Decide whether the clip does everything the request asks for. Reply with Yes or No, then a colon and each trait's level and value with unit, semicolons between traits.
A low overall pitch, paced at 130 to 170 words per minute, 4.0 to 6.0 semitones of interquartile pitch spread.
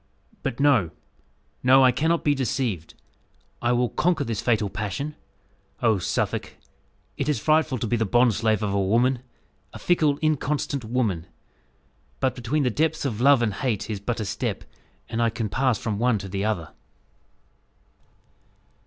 Yes: low, 120 Hz; average, 160 wpm; average, 4.3 semitones